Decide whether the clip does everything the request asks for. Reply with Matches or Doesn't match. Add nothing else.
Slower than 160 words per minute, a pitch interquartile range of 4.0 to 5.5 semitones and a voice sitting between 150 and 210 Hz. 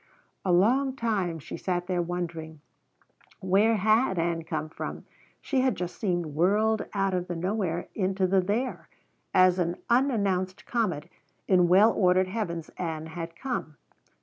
Doesn't match